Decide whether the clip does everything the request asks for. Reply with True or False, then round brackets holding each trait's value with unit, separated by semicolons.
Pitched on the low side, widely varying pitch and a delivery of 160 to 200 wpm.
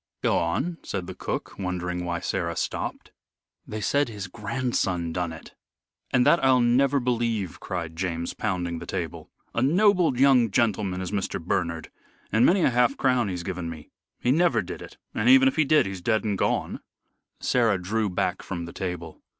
True (105 Hz; 6.1 semitones; 180 wpm)